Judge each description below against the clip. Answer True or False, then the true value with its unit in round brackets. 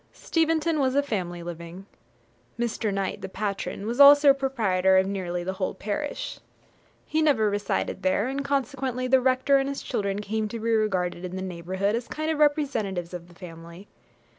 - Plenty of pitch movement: True (6.4 semitones)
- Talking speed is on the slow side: False (180 wpm)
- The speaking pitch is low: False (210 Hz)